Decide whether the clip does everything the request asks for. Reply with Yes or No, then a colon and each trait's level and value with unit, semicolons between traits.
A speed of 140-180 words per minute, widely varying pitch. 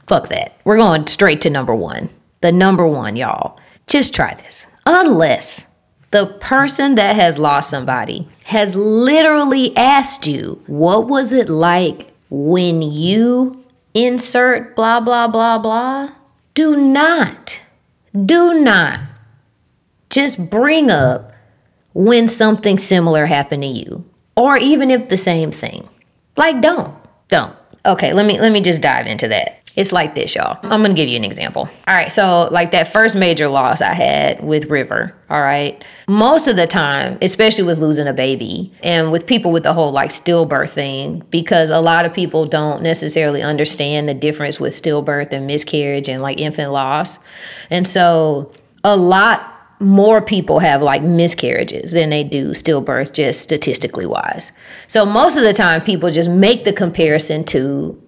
Yes: average, 160 wpm; wide, 7.1 semitones